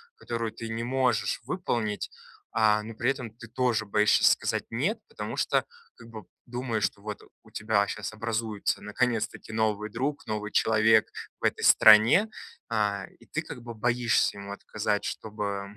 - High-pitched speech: No, low, 110 Hz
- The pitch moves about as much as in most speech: No, narrow, 2.1 semitones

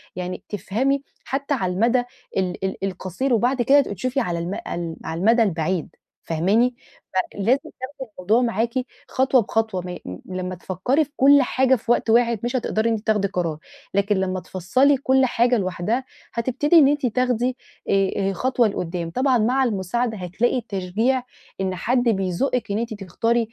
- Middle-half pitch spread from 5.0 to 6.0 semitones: Yes, average, 5.3 semitones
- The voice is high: Yes, high, 225 Hz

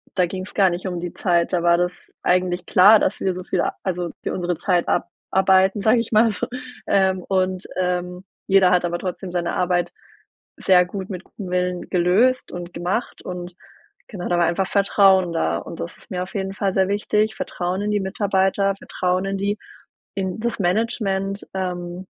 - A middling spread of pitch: No, narrow, 1.7 semitones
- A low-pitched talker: No, medium, 185 Hz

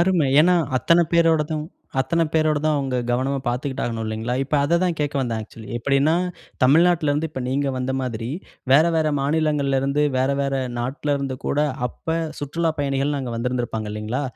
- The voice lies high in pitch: No, medium, 140 Hz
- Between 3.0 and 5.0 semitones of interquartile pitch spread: Yes, average, 3.5 semitones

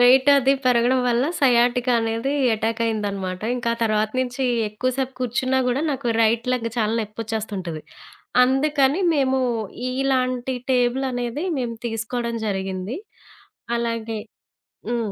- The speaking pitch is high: Yes, high, 240 Hz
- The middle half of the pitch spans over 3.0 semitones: No, average, 2.7 semitones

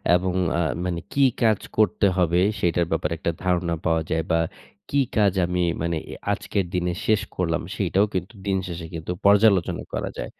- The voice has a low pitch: Yes, very low, 90 Hz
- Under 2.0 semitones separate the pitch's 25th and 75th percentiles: No, average, 2.7 semitones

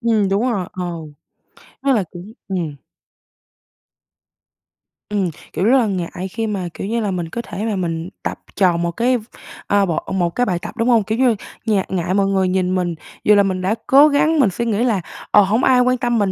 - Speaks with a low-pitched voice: No, high, 200 Hz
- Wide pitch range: No, average, 4.2 semitones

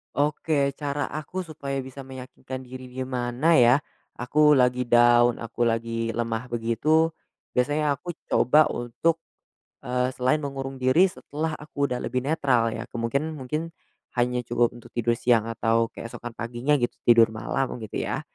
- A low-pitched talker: Yes, low, 125 Hz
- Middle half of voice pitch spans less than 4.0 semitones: Yes, average, 3.3 semitones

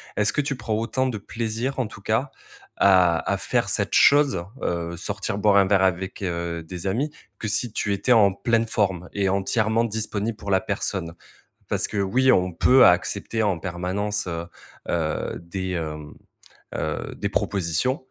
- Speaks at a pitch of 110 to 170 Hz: No, low, 100 Hz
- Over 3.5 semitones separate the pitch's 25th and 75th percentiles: Yes, average, 3.9 semitones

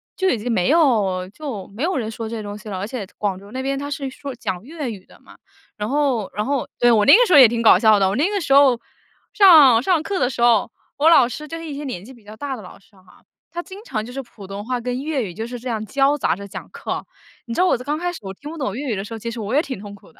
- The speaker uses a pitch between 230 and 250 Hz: Yes, high, 245 Hz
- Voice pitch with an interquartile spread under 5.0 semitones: No, average, 5.3 semitones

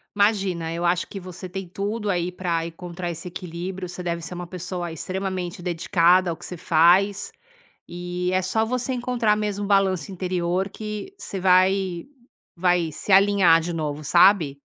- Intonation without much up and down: Yes, narrow, 2.2 semitones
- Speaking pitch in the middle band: Yes, medium, 180 Hz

